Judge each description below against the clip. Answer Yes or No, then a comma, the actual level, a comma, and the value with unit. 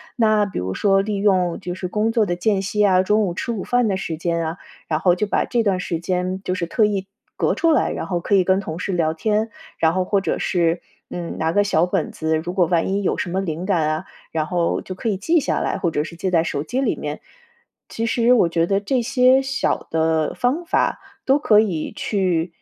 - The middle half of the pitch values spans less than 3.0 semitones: No, average, 3.8 semitones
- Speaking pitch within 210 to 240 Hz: No, medium, 185 Hz